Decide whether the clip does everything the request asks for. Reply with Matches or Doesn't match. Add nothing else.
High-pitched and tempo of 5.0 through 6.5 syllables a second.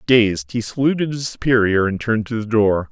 Doesn't match